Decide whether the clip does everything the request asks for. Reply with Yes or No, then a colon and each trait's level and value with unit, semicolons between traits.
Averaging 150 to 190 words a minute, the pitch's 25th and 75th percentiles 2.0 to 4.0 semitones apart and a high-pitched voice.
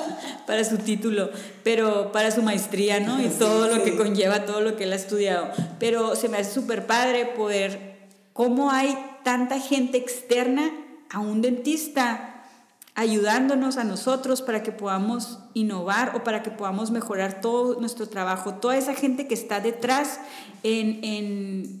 Yes: average, 155 wpm; average, 3.4 semitones; high, 225 Hz